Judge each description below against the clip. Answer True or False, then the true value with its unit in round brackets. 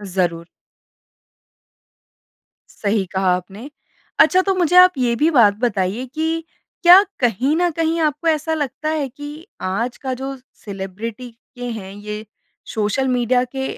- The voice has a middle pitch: False (245 Hz)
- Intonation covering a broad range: True (6.6 semitones)